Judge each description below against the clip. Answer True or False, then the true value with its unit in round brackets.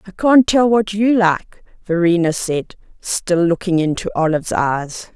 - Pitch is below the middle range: False (185 Hz)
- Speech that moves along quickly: False (150 wpm)